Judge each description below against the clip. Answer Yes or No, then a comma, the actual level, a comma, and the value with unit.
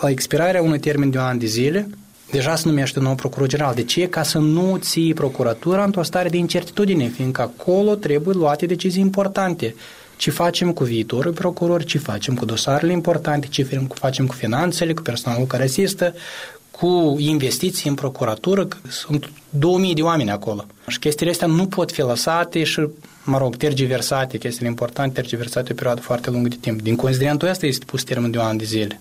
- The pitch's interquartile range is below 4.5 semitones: No, wide, 5.5 semitones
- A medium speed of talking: No, fast, 190 wpm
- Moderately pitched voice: Yes, medium, 145 Hz